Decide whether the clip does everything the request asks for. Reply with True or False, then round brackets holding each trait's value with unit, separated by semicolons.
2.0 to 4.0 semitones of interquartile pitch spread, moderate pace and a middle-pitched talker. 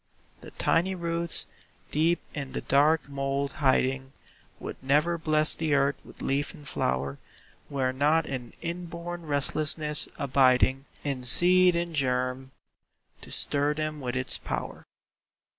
False (3.5 semitones; 130 wpm; 145 Hz)